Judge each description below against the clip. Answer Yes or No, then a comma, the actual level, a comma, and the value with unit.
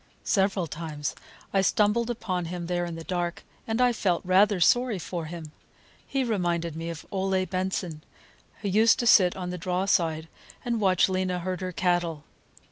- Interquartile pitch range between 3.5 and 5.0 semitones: No, average, 2.7 semitones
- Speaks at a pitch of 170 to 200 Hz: Yes, medium, 185 Hz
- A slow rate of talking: No, average, 175 wpm